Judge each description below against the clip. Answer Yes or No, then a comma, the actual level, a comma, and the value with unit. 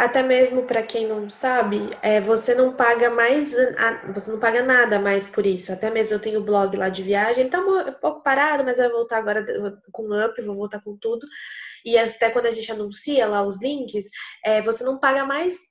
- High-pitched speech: Yes, high, 230 Hz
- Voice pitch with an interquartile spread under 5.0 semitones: Yes, average, 3.4 semitones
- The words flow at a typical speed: No, fast, 220 wpm